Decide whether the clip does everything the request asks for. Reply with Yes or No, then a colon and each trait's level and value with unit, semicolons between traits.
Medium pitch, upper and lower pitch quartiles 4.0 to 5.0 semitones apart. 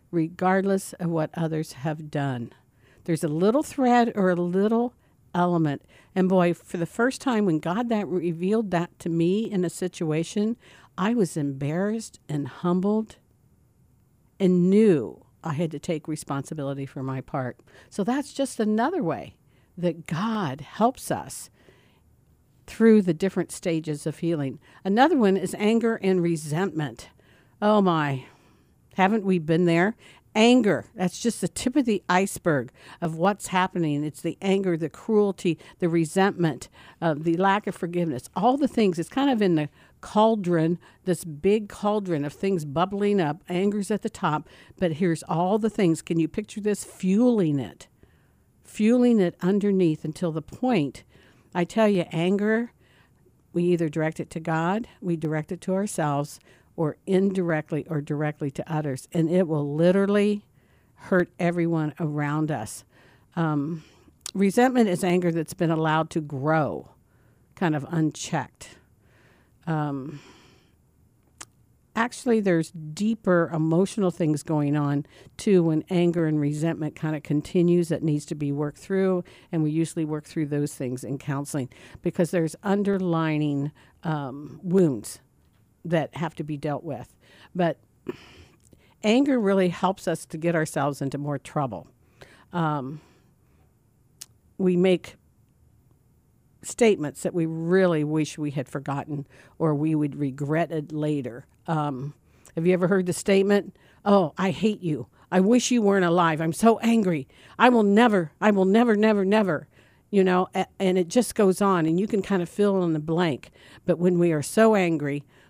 Yes: medium, 170 Hz; average, 4.3 semitones